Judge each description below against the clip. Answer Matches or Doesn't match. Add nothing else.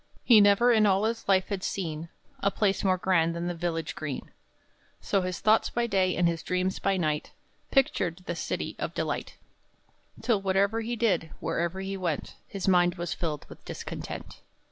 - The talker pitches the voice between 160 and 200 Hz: Matches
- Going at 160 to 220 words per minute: Matches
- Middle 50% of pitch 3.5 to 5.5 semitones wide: Doesn't match